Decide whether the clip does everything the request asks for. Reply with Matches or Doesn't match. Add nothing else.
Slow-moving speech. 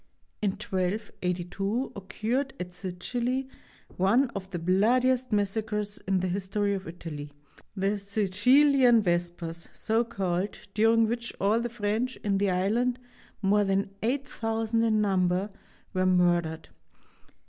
Matches